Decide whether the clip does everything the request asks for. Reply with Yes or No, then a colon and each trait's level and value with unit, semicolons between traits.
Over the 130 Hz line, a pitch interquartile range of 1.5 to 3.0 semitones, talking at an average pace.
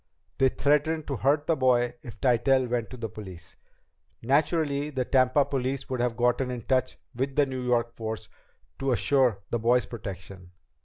No: low, 125 Hz; average, 2.7 semitones; average, 170 wpm